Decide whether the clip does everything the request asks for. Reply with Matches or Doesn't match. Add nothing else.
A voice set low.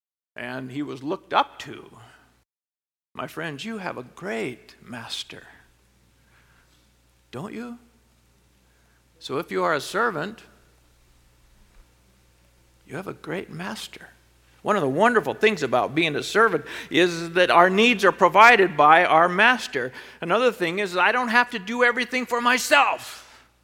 Doesn't match